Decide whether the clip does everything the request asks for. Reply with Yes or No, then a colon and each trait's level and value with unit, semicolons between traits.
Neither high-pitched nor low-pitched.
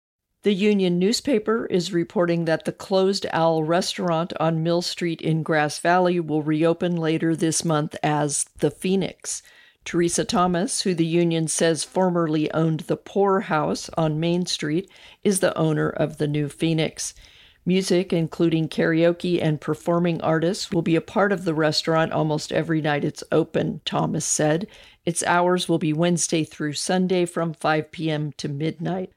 Yes: medium, 165 Hz